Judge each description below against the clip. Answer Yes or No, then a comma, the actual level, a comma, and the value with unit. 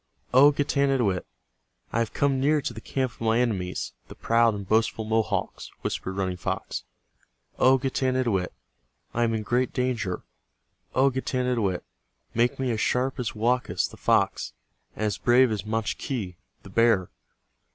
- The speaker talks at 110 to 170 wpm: Yes, average, 150 wpm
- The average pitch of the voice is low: Yes, low, 115 Hz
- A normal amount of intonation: Yes, average, 3.2 semitones